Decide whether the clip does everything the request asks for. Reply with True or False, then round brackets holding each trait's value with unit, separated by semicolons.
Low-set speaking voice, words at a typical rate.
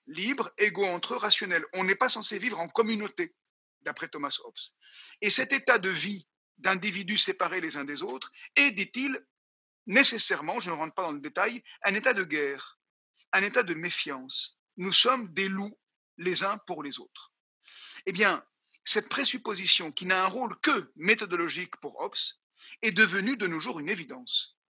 False (205 Hz; 175 wpm)